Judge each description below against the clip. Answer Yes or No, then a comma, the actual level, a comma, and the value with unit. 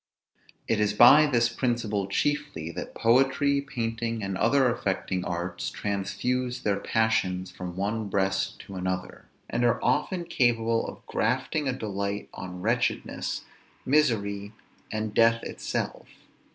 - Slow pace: Yes, slow, 125 wpm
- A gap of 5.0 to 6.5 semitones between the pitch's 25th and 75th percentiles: No, average, 4.1 semitones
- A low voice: Yes, low, 115 Hz